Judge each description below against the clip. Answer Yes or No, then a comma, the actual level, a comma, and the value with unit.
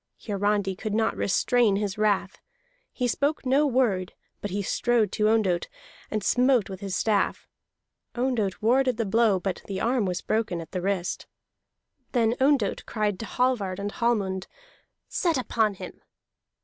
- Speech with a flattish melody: No, average, 3.7 semitones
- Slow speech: No, average, 150 wpm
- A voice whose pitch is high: Yes, high, 215 Hz